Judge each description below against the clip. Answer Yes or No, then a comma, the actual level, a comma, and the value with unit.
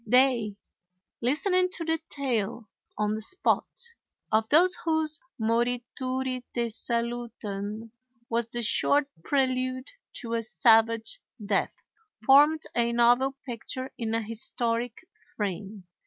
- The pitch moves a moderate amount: Yes, average, 3.1 semitones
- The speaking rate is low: Yes, slow, 110 wpm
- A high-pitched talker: Yes, high, 240 Hz